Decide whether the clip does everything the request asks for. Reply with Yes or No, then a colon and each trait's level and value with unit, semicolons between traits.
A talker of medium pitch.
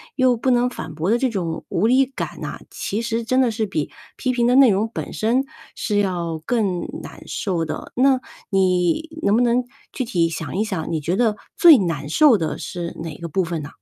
No: high, 210 Hz